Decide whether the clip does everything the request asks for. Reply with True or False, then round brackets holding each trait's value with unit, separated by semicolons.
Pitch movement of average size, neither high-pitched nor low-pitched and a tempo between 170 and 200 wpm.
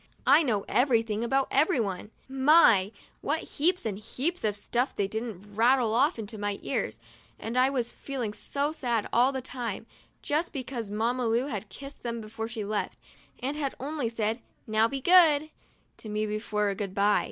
False (4.3 semitones; 235 Hz; 180 wpm)